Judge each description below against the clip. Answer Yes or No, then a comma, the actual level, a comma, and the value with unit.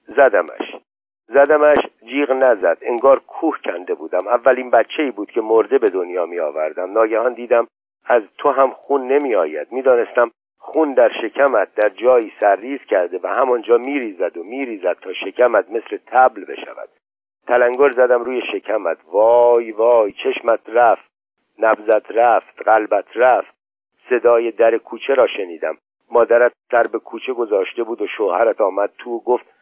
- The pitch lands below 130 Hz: No, medium, 140 Hz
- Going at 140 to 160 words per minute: Yes, average, 150 wpm